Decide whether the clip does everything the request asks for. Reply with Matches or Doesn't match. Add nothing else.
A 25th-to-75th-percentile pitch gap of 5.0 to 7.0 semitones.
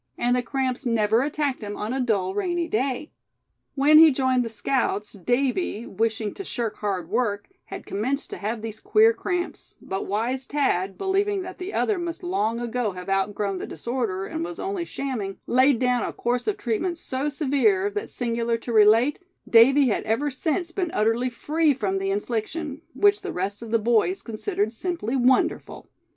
Matches